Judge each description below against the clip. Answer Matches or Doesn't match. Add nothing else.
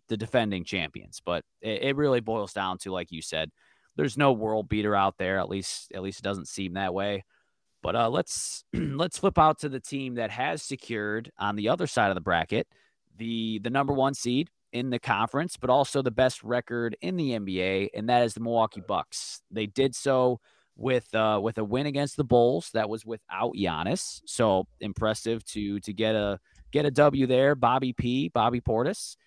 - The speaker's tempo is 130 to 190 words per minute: Doesn't match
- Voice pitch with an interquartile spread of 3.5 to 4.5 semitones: Matches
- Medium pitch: Doesn't match